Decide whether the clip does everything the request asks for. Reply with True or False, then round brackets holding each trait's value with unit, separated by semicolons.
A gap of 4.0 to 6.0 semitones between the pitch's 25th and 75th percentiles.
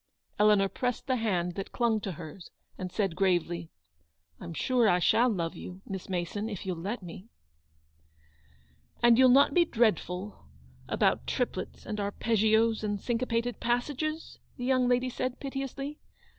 True (4.9 semitones)